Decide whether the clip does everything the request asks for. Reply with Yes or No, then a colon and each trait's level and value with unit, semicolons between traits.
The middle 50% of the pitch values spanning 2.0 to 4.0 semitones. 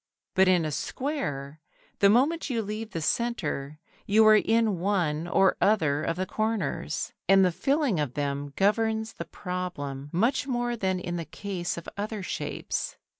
No: average, 5.3 semitones